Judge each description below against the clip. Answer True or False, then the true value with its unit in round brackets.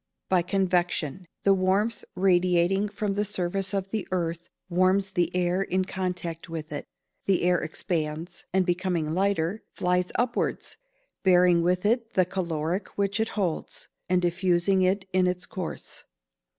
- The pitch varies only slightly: True (1.9 semitones)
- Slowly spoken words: False (150 wpm)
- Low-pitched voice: False (185 Hz)